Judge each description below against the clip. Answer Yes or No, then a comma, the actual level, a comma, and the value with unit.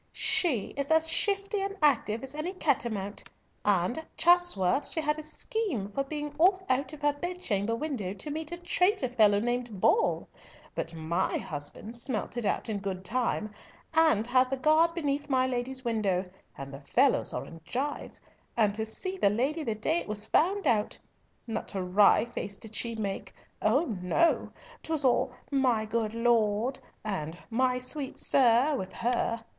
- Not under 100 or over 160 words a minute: No, average, 175 wpm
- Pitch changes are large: Yes, wide, 6.3 semitones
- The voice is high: Yes, high, 245 Hz